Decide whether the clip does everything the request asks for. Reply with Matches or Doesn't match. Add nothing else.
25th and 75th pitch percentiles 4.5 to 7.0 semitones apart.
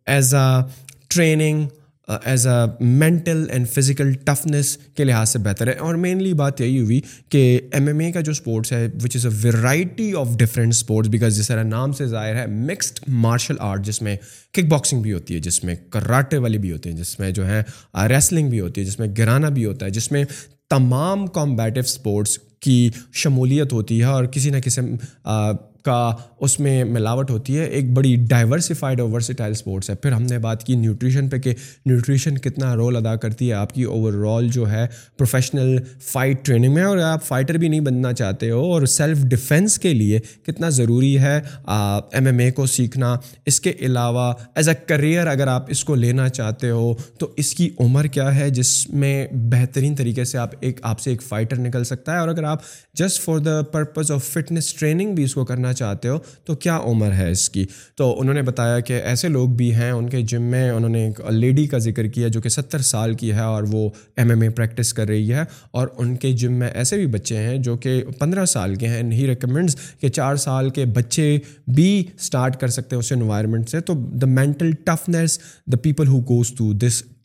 Doesn't match